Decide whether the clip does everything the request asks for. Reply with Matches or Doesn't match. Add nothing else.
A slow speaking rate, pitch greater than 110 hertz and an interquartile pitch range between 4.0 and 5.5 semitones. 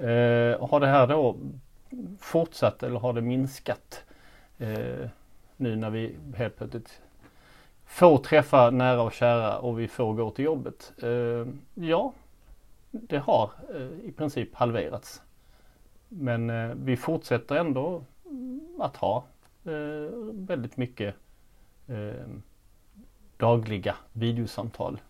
Matches